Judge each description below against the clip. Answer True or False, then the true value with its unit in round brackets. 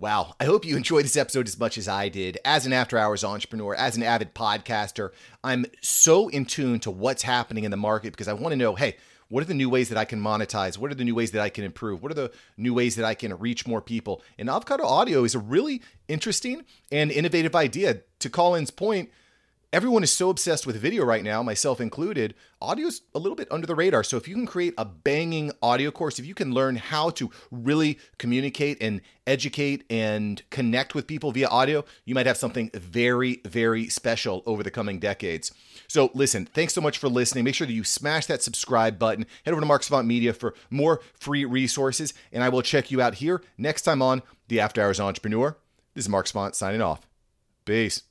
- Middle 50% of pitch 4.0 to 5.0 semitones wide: True (4.7 semitones)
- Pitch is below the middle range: True (125 Hz)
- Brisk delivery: True (220 wpm)